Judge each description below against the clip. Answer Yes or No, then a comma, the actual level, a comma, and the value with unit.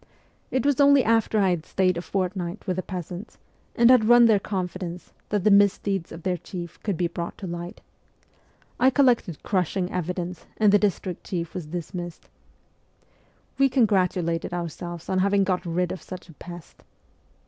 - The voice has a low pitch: No, medium, 185 Hz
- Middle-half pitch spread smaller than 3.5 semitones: Yes, average, 3.0 semitones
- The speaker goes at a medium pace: Yes, average, 175 wpm